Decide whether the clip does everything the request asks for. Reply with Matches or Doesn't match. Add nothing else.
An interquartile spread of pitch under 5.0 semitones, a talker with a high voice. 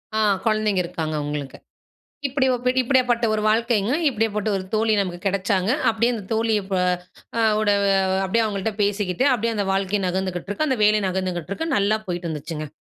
Matches